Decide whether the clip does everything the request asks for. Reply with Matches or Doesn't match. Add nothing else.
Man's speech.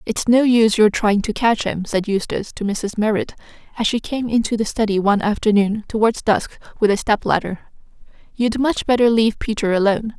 Doesn't match